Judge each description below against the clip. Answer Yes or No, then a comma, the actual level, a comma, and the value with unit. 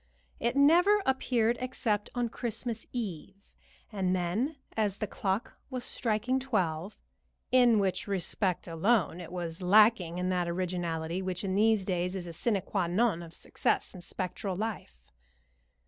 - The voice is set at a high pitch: Yes, high, 195 Hz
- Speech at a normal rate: Yes, average, 145 wpm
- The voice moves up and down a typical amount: Yes, average, 4.7 semitones